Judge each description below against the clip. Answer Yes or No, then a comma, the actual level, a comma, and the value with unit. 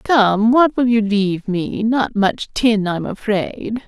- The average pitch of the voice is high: Yes, high, 220 Hz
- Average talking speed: Yes, average, 170 wpm